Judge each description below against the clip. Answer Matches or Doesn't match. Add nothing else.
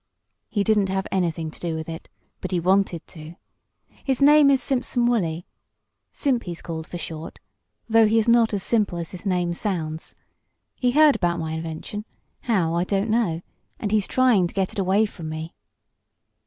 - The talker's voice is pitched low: Doesn't match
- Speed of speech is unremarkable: Matches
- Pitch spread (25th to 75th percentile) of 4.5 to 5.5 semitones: Matches